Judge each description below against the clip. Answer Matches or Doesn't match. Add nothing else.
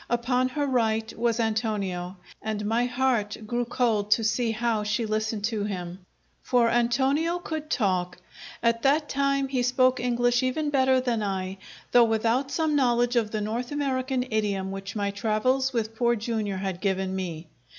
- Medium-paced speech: Matches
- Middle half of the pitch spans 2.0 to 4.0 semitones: Matches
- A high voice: Matches